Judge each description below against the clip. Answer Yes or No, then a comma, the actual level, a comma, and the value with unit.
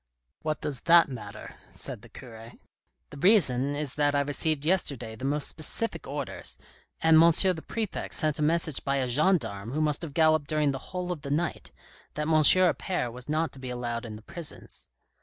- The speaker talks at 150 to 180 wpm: No, average, 195 wpm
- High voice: No, medium, 150 Hz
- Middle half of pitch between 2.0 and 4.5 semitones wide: Yes, average, 4.0 semitones